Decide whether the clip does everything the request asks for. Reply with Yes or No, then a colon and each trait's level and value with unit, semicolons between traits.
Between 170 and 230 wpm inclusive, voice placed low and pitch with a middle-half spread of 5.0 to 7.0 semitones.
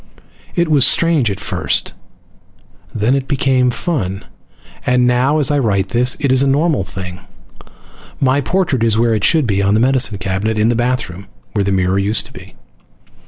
Yes: average, 180 wpm; low, 120 Hz; wide, 5.4 semitones